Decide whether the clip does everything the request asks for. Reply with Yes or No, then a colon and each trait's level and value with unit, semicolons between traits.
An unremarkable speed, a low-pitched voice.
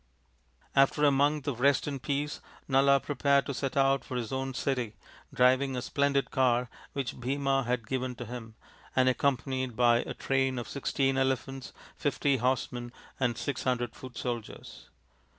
Yes: average, 160 wpm; low, 130 Hz